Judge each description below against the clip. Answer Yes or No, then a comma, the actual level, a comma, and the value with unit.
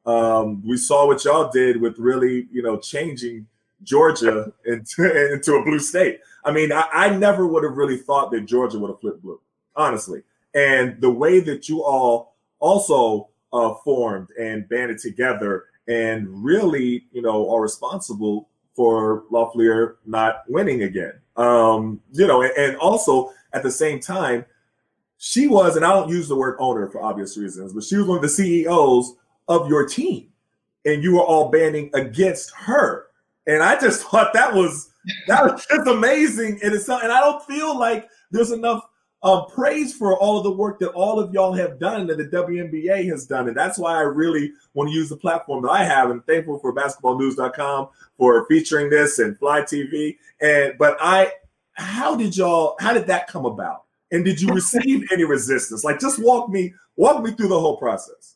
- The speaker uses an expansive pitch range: Yes, wide, 7.7 semitones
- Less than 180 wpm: No, average, 185 wpm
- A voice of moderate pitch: Yes, medium, 150 Hz